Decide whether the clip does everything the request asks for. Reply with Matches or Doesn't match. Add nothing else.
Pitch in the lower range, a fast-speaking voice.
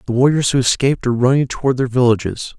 Matches